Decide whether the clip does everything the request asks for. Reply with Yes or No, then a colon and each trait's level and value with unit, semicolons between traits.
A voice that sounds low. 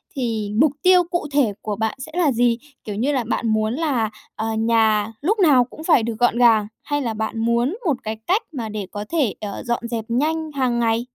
No: high, 235 Hz